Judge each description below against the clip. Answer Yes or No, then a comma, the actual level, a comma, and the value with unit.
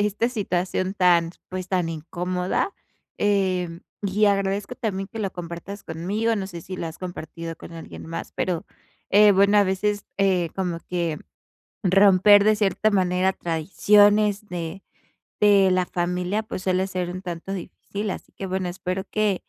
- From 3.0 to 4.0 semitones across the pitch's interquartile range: No, narrow, 2.4 semitones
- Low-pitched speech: No, high, 190 Hz